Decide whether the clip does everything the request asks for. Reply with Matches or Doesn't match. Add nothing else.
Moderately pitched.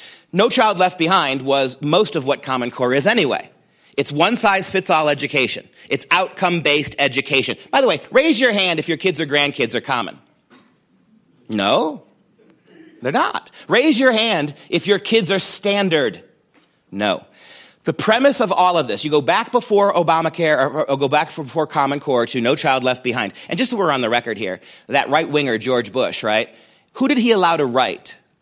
Matches